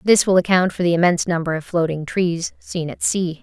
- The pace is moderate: No, fast, 230 wpm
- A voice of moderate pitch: Yes, medium, 175 Hz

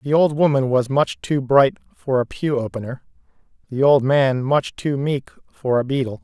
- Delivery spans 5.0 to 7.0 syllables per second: No, 4.6 syllables/s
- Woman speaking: No, male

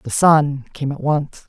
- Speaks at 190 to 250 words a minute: Yes, fast, 205 wpm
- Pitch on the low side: No, medium, 145 Hz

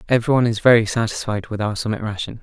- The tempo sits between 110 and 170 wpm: No, average, 200 wpm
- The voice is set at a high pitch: No, low, 110 Hz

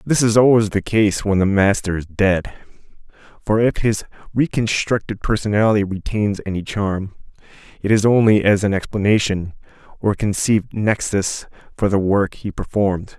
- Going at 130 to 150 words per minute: Yes, average, 145 wpm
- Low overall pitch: Yes, low, 105 Hz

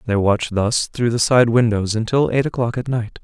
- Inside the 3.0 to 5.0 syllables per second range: No, 5.3 syllables/s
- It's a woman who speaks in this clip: No, male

